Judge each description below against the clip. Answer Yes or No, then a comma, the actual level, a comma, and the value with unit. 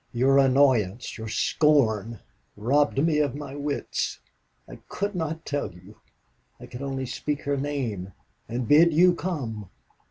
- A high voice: No, medium, 140 Hz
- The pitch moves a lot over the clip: No, average, 4.3 semitones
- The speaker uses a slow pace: No, average, 145 wpm